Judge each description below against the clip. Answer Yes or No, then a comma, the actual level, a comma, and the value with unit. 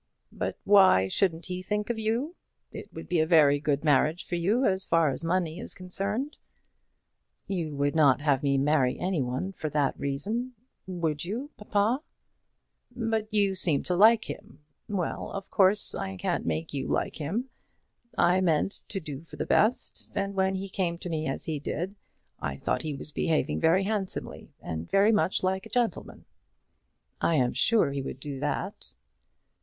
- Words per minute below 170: No, average, 175 wpm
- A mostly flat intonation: No, wide, 5.5 semitones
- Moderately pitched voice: Yes, medium, 180 Hz